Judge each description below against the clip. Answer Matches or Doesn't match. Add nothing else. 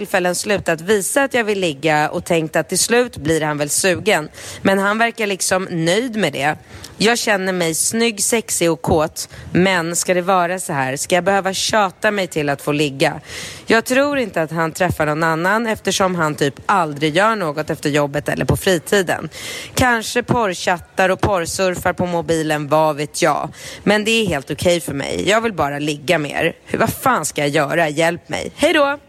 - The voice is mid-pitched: Matches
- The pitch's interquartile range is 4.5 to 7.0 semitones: Matches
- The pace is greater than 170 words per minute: Matches